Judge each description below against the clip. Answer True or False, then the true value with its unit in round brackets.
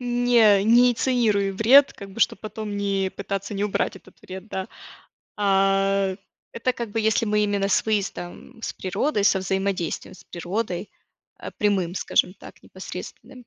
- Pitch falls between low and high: False (200 Hz)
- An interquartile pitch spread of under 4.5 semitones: True (2.7 semitones)